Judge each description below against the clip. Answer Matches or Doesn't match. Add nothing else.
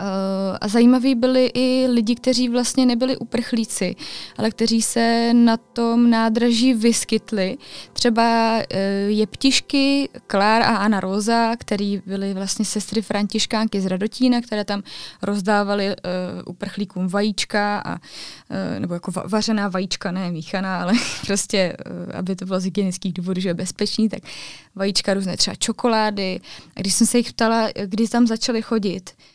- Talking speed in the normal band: Matches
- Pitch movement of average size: Matches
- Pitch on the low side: Doesn't match